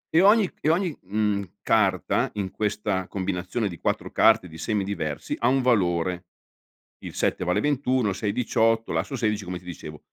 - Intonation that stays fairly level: No, average, 4.7 semitones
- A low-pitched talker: Yes, low, 105 Hz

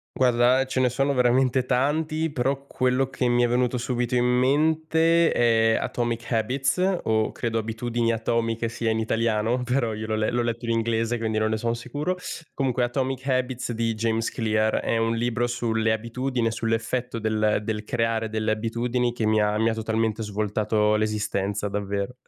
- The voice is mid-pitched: No, low, 115 Hz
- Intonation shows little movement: Yes, narrow, 2.3 semitones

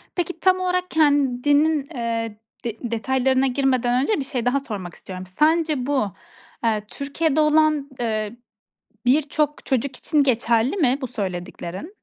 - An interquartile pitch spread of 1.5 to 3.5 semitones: No, average, 4.7 semitones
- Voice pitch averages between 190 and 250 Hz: No, very high, 265 Hz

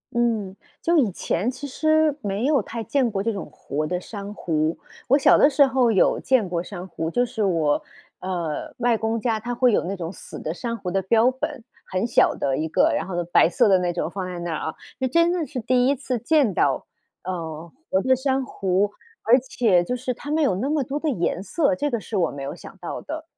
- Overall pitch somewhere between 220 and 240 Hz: Yes, high, 225 Hz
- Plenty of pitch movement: Yes, wide, 6.3 semitones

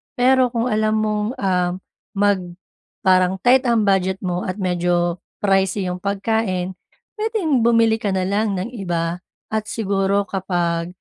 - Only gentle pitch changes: No, average, 3.3 semitones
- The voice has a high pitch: Yes, high, 195 Hz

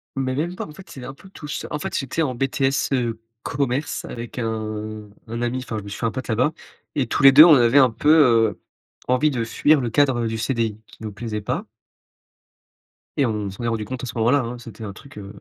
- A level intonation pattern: No, average, 3.5 semitones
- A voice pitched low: Yes, low, 120 Hz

